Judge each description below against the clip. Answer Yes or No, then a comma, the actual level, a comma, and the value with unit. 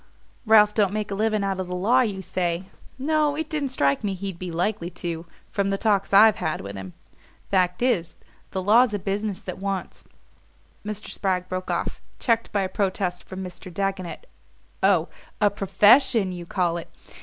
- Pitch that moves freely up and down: No, average, 2.9 semitones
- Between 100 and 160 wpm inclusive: No, average, 185 wpm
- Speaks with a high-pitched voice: Yes, high, 195 Hz